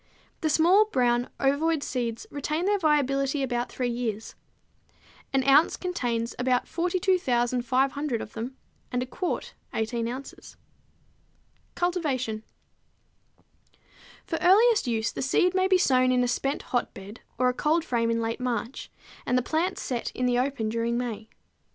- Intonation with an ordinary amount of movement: Yes, average, 4.7 semitones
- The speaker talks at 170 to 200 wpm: No, average, 145 wpm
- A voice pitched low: No, very high, 255 Hz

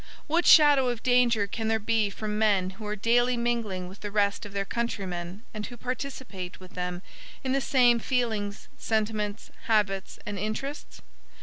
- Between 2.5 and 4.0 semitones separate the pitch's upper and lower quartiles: Yes, average, 3.2 semitones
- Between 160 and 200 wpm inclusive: Yes, average, 170 wpm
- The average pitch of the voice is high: Yes, high, 215 Hz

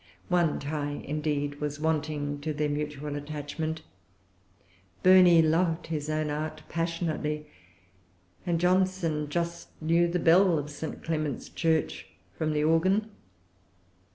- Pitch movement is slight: Yes, narrow, 2.2 semitones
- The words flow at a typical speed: No, slow, 120 wpm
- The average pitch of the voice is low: No, medium, 155 Hz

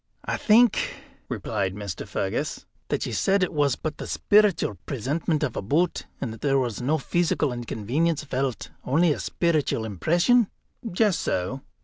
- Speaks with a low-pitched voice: No, medium, 145 Hz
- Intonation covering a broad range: Yes, wide, 6.4 semitones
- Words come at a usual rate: Yes, average, 155 wpm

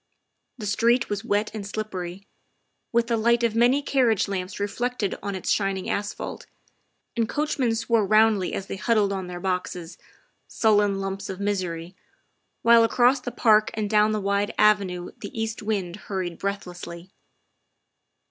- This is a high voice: Yes, high, 205 Hz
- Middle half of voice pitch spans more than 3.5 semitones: No, average, 2.9 semitones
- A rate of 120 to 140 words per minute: No, average, 150 wpm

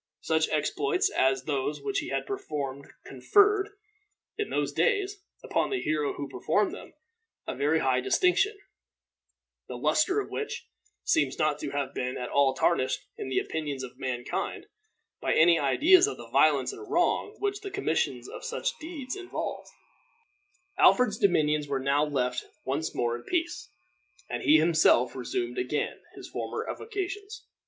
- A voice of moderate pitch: Yes, medium, 160 Hz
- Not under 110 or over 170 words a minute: Yes, average, 155 wpm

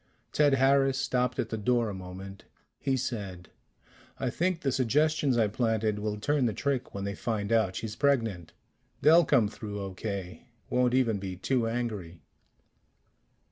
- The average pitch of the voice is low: Yes, low, 115 Hz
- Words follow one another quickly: No, average, 155 wpm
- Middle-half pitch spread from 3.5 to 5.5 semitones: Yes, average, 4.6 semitones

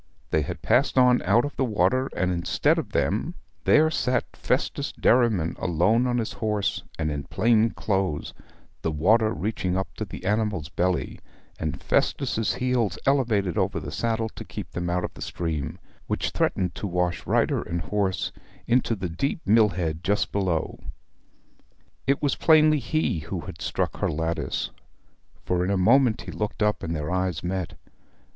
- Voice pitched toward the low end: Yes, low, 100 Hz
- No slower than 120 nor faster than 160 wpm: No, average, 170 wpm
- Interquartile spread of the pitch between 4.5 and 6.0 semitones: Yes, average, 5.2 semitones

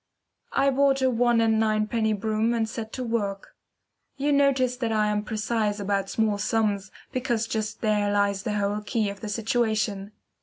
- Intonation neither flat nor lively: No, narrow, 2.2 semitones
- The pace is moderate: Yes, average, 175 wpm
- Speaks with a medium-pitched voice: No, high, 220 Hz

